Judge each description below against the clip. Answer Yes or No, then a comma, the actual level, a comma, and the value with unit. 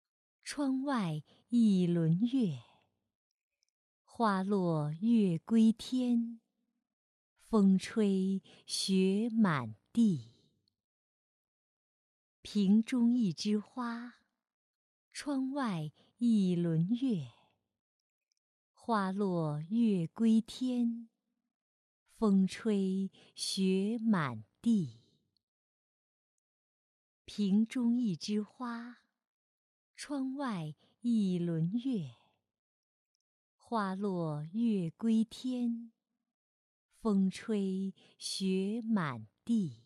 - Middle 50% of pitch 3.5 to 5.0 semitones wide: No, wide, 5.5 semitones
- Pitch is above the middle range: Yes, high, 210 Hz